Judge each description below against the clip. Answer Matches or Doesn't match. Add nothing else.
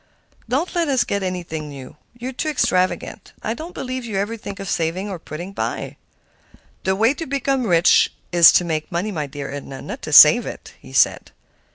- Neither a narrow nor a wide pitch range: Doesn't match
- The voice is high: Matches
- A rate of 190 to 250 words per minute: Matches